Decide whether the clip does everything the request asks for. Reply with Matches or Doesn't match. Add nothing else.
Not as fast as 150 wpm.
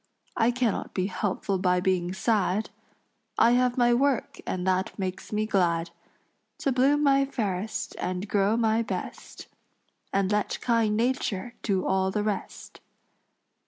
Matches